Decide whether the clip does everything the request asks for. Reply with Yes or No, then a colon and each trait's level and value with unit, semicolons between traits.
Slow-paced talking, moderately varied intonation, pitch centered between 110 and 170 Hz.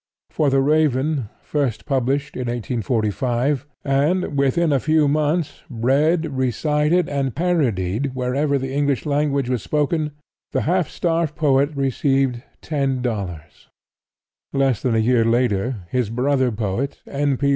Yes: slow, 130 wpm; average, 3.2 semitones; low, 135 Hz